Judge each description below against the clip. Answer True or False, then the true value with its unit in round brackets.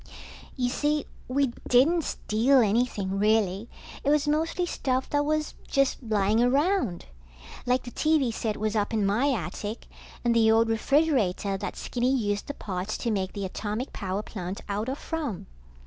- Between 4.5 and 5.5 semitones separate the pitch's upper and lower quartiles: True (5.1 semitones)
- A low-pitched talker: False (235 Hz)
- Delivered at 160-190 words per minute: True (165 wpm)